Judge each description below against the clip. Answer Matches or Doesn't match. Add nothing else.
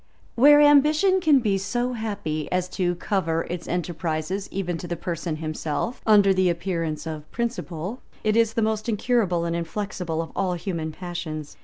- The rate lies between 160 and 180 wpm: Matches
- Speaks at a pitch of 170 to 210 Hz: Matches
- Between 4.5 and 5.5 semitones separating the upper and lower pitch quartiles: Matches